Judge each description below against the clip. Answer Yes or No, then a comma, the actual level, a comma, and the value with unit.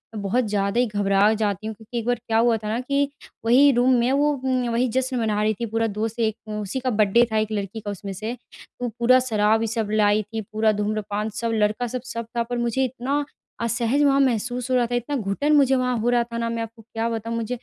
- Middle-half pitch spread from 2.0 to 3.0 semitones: Yes, narrow, 2.6 semitones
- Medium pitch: No, high, 230 Hz